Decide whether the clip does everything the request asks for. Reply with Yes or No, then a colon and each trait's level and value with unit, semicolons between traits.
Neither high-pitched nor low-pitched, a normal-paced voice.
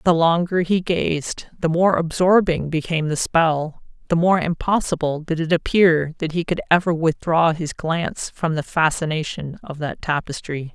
Yes: medium, 165 Hz; average, 155 wpm